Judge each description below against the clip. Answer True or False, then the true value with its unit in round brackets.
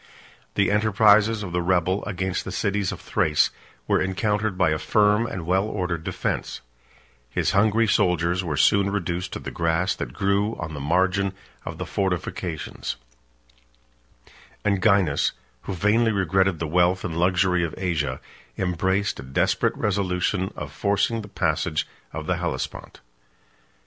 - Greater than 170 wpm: False (145 wpm)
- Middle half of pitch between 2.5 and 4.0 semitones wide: True (2.8 semitones)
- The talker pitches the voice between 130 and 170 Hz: False (95 Hz)